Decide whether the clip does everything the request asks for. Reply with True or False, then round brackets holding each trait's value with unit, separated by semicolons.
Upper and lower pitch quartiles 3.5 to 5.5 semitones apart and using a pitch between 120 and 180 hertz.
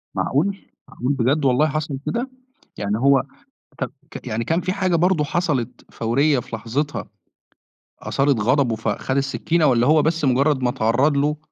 True (4.0 semitones; 140 Hz)